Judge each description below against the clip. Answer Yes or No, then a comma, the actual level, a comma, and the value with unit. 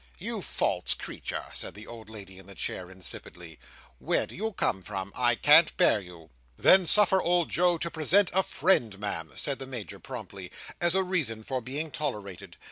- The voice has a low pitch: Yes, low, 120 Hz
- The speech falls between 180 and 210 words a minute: Yes, average, 185 wpm